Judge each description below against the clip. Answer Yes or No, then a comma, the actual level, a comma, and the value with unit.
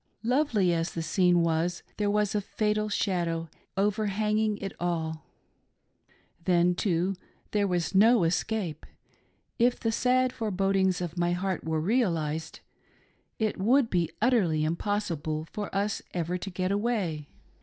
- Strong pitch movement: No, average, 3.9 semitones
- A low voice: No, high, 190 Hz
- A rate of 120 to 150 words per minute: Yes, slow, 135 wpm